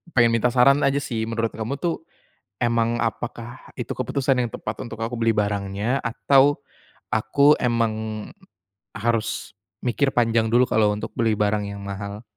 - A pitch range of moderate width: No, narrow, 2.2 semitones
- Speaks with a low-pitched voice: Yes, low, 115 Hz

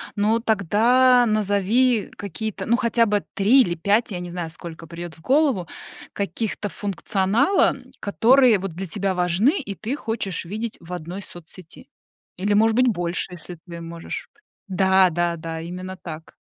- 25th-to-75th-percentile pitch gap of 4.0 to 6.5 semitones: Yes, average, 4.3 semitones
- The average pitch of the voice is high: Yes, high, 195 Hz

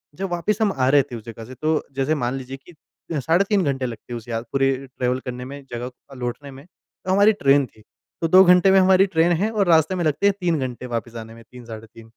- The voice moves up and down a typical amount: No, wide, 6.1 semitones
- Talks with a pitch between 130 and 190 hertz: Yes, medium, 140 Hz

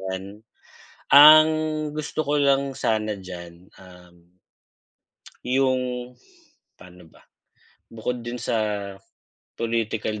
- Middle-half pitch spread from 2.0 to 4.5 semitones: No, wide, 5.5 semitones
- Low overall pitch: Yes, low, 110 Hz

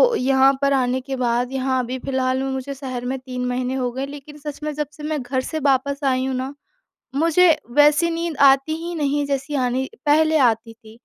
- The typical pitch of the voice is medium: No, very high, 270 Hz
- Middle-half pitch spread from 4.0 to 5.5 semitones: No, narrow, 2.4 semitones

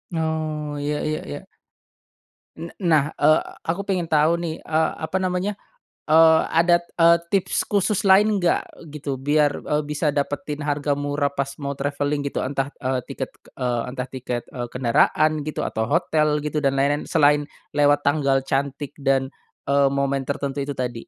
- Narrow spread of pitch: Yes, narrow, 2.3 semitones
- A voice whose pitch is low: No, medium, 145 Hz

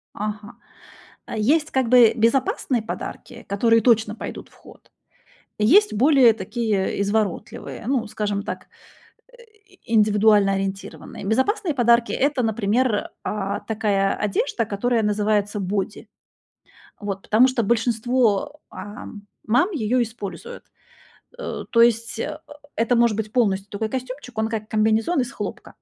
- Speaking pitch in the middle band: No, high, 220 Hz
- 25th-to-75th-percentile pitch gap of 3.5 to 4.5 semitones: No, average, 3.0 semitones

